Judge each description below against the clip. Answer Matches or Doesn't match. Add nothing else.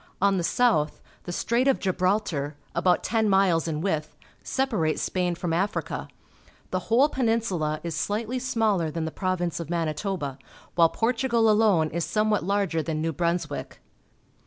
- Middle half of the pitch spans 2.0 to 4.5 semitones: Doesn't match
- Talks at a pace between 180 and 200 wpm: Doesn't match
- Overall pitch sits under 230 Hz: Matches